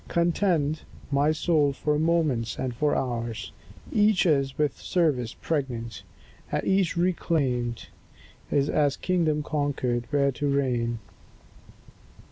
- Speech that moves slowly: Yes, slow, 110 wpm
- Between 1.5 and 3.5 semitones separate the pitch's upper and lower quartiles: No, average, 4.4 semitones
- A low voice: No, medium, 145 Hz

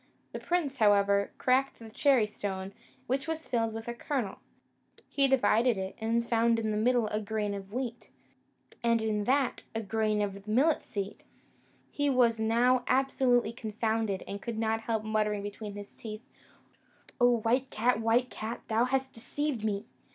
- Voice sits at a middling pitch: No, high, 225 Hz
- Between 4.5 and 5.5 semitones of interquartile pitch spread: No, average, 2.9 semitones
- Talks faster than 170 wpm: No, average, 165 wpm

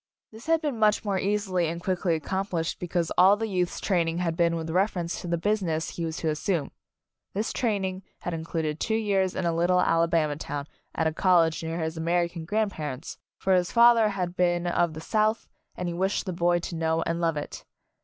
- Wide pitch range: No, average, 2.9 semitones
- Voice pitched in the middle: Yes, medium, 175 Hz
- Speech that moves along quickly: Yes, fast, 215 wpm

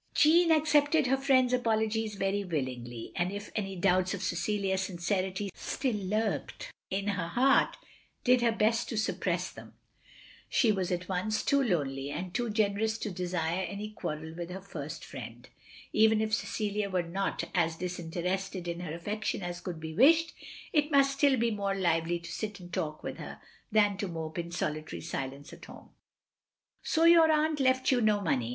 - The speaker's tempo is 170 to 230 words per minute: Yes, average, 180 wpm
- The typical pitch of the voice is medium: No, high, 195 Hz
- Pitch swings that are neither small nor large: Yes, average, 4.5 semitones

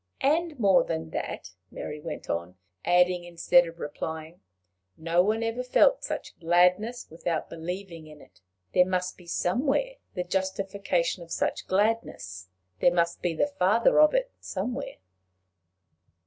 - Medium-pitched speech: Yes, medium, 180 Hz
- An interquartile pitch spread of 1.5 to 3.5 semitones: No, average, 4.8 semitones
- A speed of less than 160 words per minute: Yes, average, 140 wpm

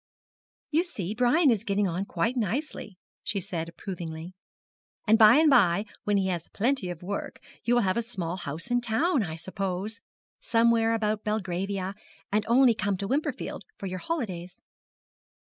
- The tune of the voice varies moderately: Yes, average, 4.3 semitones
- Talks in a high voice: Yes, high, 205 Hz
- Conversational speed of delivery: Yes, average, 160 wpm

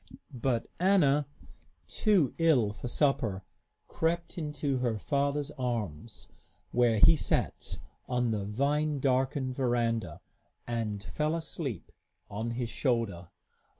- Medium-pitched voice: No, low, 125 Hz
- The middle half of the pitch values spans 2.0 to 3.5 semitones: No, average, 4.4 semitones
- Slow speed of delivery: Yes, slow, 110 wpm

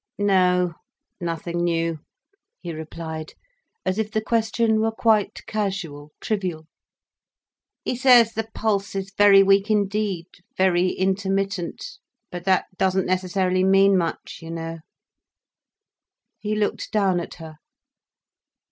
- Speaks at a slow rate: Yes, slow, 110 wpm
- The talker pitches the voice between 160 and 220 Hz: Yes, high, 190 Hz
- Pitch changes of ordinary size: Yes, average, 3.2 semitones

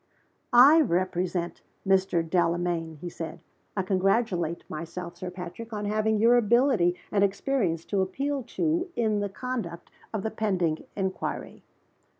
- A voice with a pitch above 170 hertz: Yes, high, 190 Hz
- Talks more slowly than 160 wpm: Yes, slow, 135 wpm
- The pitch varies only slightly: No, average, 4.2 semitones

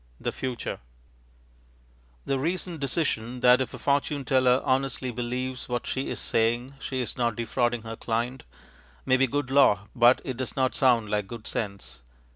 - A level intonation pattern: Yes, narrow, 2.2 semitones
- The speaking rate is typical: Yes, average, 165 wpm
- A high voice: No, low, 125 Hz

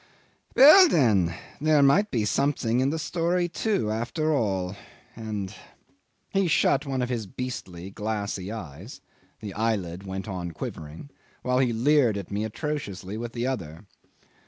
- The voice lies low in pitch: Yes, low, 115 Hz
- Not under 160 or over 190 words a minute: No, average, 150 wpm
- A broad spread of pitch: Yes, wide, 6.4 semitones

